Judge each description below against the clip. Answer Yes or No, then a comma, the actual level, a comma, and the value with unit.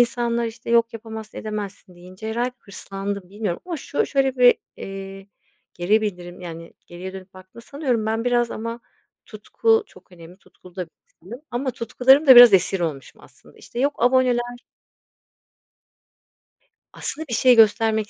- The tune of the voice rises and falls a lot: No, average, 4.3 semitones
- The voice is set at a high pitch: Yes, high, 220 Hz